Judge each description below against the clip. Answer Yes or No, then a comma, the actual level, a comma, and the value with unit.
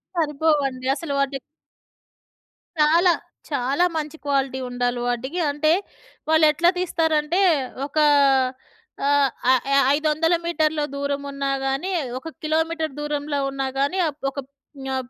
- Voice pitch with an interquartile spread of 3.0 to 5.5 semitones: No, narrow, 2.6 semitones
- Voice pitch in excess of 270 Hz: Yes, very high, 290 Hz